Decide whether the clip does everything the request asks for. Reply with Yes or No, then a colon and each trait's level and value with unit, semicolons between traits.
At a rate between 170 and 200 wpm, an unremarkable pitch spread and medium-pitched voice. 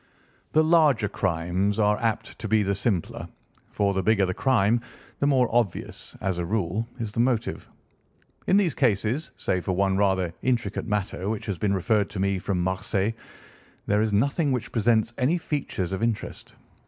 No: average, 175 wpm; average, 3.5 semitones; low, 105 Hz